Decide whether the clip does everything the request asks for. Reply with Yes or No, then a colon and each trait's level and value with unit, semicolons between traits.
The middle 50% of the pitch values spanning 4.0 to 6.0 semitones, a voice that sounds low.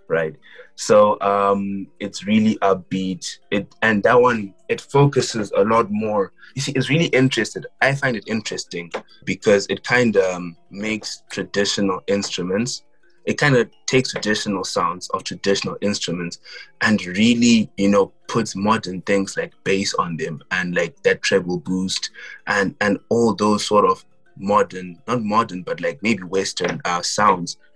No: average, 3.0 semitones; low, 105 Hz